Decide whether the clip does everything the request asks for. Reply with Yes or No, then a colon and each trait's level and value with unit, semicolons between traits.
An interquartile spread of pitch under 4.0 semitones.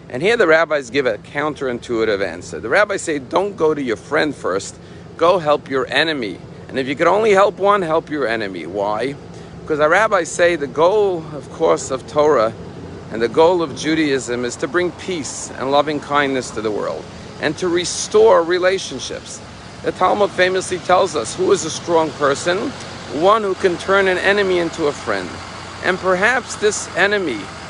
No: average, 4.8 semitones